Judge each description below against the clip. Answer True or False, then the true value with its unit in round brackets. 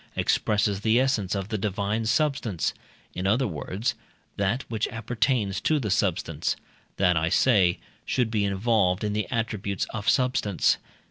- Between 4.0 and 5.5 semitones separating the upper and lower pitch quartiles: False (3.1 semitones)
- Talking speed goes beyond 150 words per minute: False (140 wpm)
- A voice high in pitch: False (105 Hz)